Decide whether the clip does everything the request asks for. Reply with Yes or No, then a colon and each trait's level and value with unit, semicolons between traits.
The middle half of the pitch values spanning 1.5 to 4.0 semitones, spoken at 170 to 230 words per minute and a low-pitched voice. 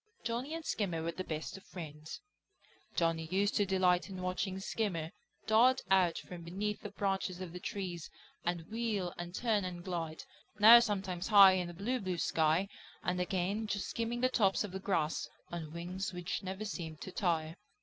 No: average, 3.0 semitones; average, 180 wpm; medium, 185 Hz